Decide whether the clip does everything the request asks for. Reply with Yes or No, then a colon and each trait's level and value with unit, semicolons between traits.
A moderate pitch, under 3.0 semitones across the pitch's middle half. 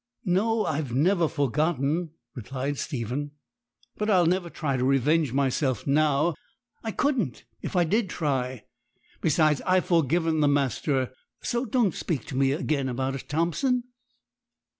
No: medium, 150 Hz; average, 4.4 semitones